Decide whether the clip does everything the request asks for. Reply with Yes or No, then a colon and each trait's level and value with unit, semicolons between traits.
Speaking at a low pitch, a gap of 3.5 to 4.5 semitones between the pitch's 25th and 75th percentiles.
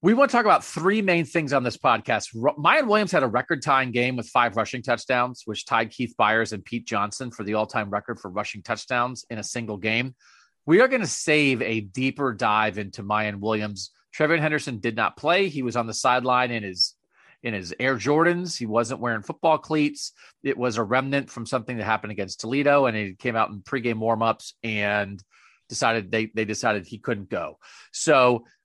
Yes: low, 120 Hz; average, 3.9 semitones